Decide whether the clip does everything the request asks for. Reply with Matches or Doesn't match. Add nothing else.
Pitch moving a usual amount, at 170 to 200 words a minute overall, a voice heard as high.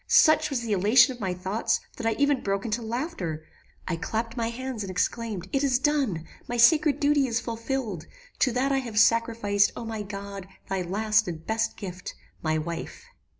Matches